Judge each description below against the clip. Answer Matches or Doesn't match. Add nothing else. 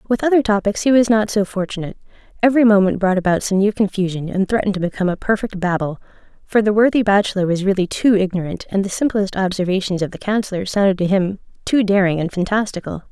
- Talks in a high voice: Matches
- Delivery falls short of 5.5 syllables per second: Doesn't match